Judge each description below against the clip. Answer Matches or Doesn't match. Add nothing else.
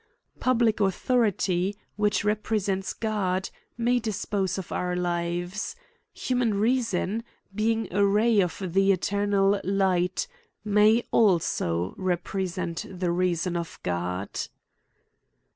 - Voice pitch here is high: Matches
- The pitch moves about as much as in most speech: Matches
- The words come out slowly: Matches